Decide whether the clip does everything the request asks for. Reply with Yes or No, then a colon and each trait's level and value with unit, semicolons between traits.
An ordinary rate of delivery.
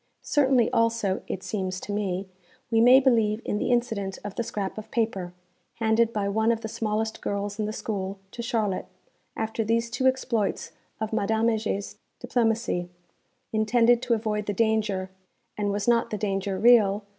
Yes: average, 170 wpm